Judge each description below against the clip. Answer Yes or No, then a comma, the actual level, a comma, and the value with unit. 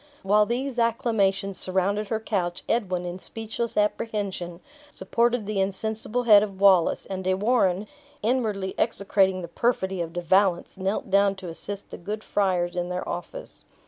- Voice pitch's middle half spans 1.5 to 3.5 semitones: Yes, average, 2.8 semitones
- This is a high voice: Yes, high, 195 Hz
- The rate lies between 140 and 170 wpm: Yes, average, 155 wpm